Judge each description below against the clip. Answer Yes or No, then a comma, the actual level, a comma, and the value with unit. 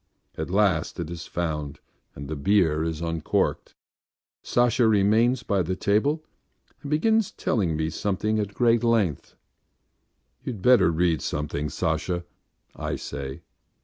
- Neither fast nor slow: No, slow, 130 wpm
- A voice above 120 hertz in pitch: No, very low, 95 Hz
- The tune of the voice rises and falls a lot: Yes, wide, 6.3 semitones